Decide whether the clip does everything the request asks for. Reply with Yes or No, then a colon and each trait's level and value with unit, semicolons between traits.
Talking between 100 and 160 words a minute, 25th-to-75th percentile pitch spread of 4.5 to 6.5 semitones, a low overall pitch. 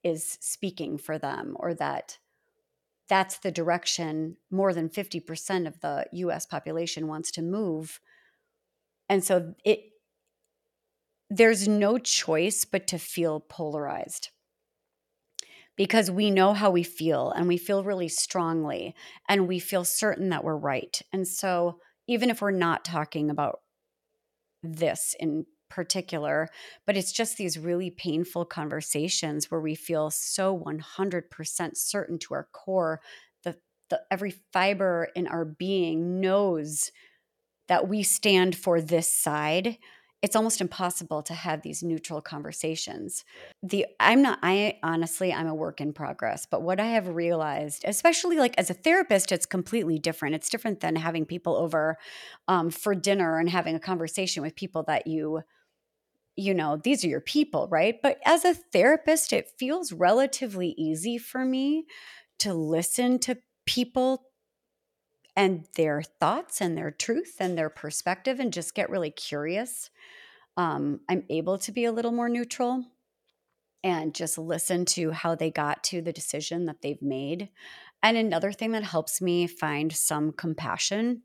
No: average, 150 wpm; wide, 5.6 semitones; medium, 185 Hz